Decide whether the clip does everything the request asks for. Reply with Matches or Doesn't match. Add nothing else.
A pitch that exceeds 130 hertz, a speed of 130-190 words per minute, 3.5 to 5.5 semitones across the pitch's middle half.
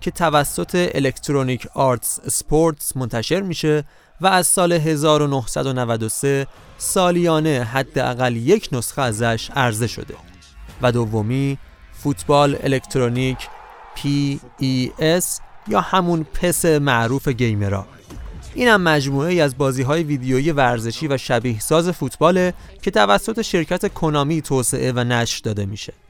Doesn't match